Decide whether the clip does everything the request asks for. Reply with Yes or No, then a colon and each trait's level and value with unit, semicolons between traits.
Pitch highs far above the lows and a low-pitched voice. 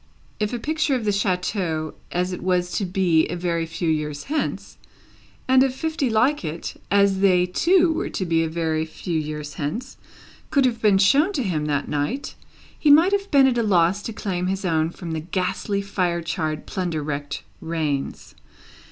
No: wide, 6.3 semitones; medium, 180 Hz